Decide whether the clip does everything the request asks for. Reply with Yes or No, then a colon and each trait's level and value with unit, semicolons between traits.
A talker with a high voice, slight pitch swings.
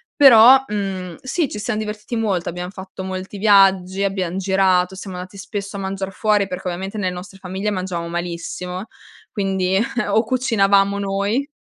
Yes: high, 195 Hz; narrow, 2.0 semitones